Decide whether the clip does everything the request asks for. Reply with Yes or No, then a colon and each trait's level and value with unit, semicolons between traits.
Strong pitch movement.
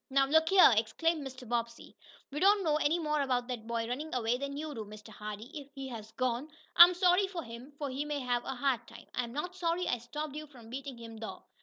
No: average, 4.6 semitones